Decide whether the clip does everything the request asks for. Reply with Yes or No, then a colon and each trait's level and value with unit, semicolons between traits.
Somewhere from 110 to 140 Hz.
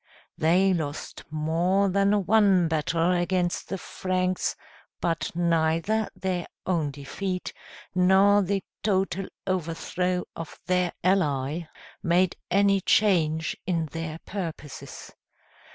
No: medium, 180 Hz